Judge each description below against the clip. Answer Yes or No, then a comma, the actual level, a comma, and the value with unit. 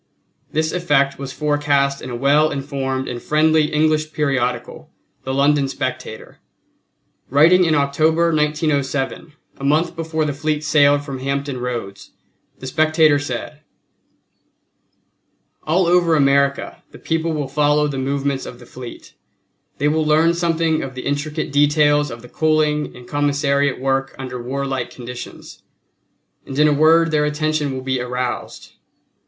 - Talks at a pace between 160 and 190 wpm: No, average, 140 wpm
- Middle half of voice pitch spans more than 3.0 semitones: No, narrow, 2.4 semitones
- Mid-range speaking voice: Yes, medium, 145 Hz